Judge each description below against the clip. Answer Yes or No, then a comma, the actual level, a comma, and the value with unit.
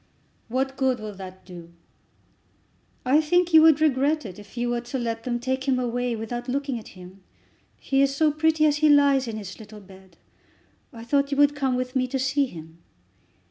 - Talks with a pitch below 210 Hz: No, very high, 255 Hz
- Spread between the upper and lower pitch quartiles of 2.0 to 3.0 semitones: No, average, 4.3 semitones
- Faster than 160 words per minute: Yes, average, 200 wpm